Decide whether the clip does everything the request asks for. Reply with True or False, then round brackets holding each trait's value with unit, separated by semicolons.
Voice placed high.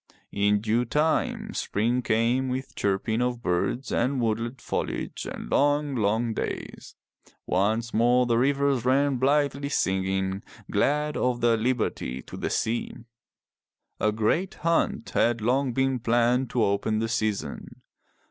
False (120 Hz)